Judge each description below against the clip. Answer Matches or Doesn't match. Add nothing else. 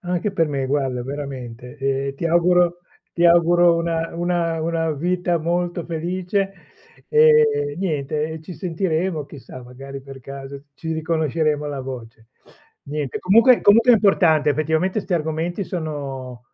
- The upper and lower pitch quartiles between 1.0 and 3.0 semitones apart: Doesn't match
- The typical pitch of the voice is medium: Matches